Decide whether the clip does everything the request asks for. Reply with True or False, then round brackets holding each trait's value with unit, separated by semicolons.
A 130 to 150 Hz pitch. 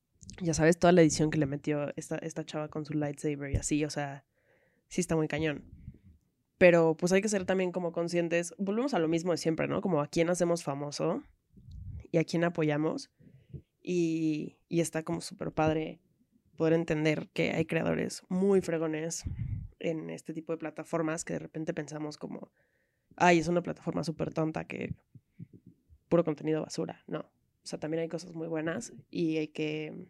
False (160 Hz)